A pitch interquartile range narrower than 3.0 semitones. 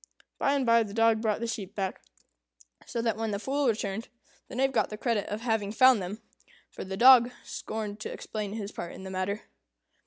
Yes: narrow, 2.4 semitones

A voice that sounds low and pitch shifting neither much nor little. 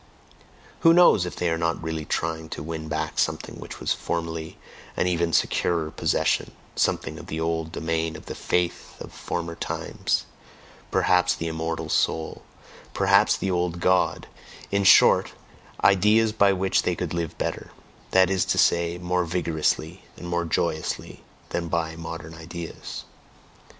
No: very low, 85 Hz; narrow, 1.9 semitones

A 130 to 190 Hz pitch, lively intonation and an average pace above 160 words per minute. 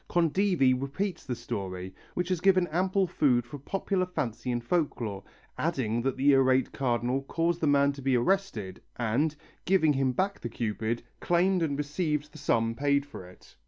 Yes: medium, 140 Hz; wide, 6.3 semitones; average, 170 wpm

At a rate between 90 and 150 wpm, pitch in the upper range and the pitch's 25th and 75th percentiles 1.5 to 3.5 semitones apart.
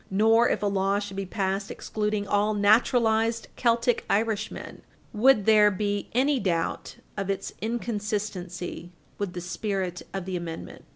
Yes: average, 140 wpm; high, 205 Hz; narrow, 2.4 semitones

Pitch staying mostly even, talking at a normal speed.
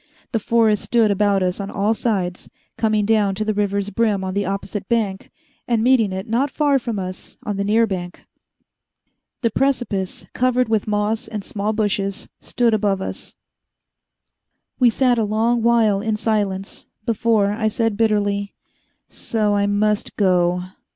Yes: narrow, 2.2 semitones; average, 160 wpm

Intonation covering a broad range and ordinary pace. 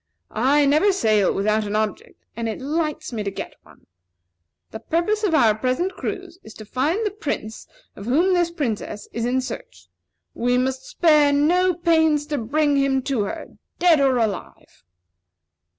Yes: wide, 6.5 semitones; average, 170 wpm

